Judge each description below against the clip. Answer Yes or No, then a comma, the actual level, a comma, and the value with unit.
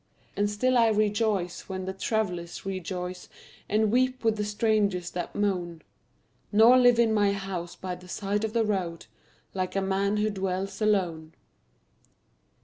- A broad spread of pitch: No, average, 2.9 semitones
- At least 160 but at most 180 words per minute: No, average, 150 wpm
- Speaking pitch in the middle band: No, high, 200 Hz